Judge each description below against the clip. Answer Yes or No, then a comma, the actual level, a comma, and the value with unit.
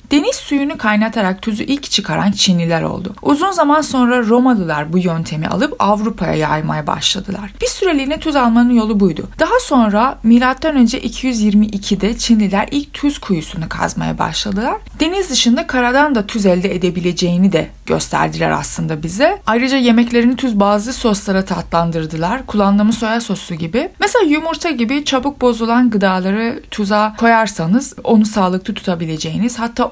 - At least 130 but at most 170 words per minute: Yes, average, 135 wpm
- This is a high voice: Yes, high, 225 Hz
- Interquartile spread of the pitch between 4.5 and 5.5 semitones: Yes, average, 5.0 semitones